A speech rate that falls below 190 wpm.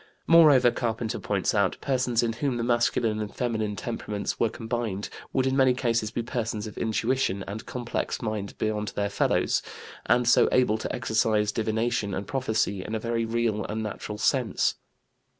Yes: average, 170 wpm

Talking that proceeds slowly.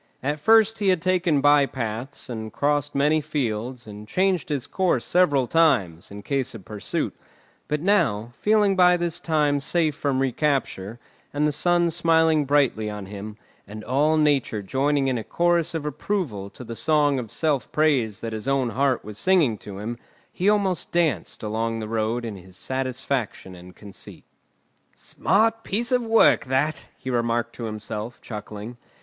No: average, 165 wpm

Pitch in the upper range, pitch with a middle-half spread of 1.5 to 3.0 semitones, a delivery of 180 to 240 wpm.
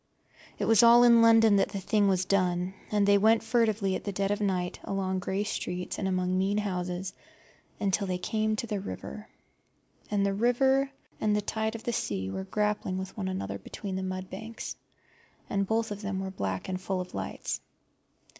Yes: high, 200 Hz; narrow, 2.6 semitones; average, 190 wpm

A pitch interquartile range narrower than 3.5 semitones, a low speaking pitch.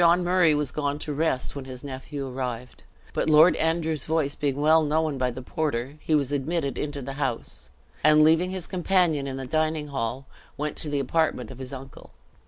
No: average, 3.0 semitones; medium, 145 Hz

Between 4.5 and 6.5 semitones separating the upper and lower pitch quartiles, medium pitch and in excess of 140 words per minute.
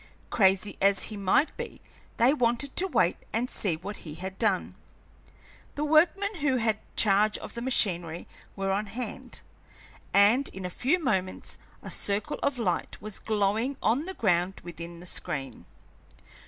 No: average, 5.1 semitones; high, 210 Hz; average, 155 wpm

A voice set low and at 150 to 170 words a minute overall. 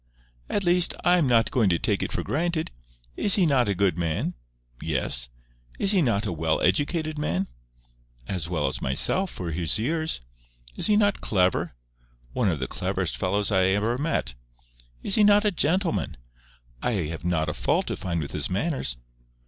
No: low, 105 Hz; average, 180 wpm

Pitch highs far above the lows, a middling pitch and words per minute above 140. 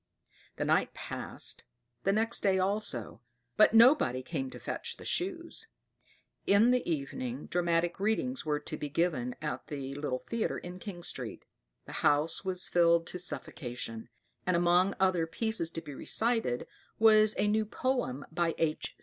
Yes: wide, 6.3 semitones; medium, 175 Hz; average, 155 wpm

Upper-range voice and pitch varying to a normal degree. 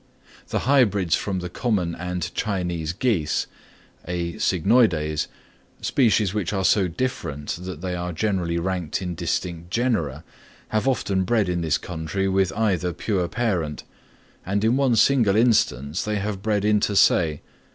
No: very low, 95 Hz; average, 3.9 semitones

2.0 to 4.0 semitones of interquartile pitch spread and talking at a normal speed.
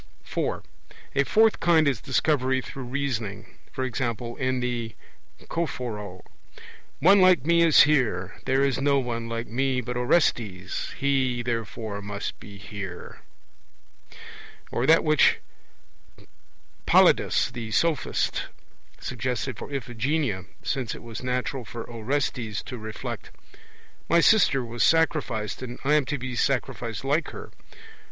No: average, 3.5 semitones; slow, 125 wpm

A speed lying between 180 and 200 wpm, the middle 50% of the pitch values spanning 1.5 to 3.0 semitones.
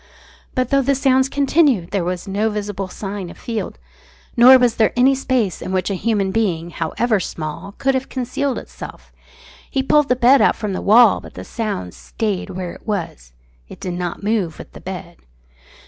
No: average, 190 wpm; wide, 5.6 semitones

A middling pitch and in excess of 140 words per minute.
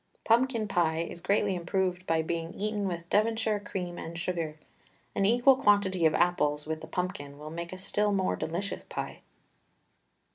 Yes: medium, 180 Hz; average, 160 wpm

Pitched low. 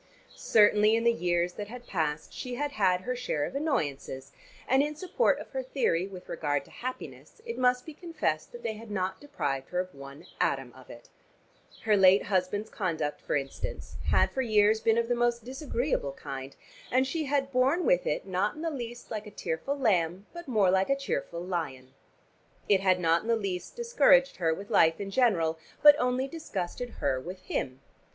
No: high, 210 Hz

